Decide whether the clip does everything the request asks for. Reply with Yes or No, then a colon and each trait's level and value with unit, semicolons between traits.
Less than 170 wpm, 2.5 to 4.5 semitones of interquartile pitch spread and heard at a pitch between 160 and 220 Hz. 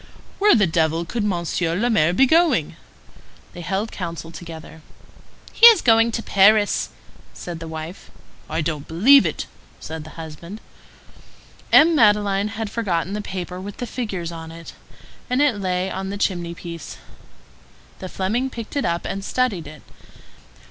No: average, 155 wpm; average, 4.9 semitones; high, 190 Hz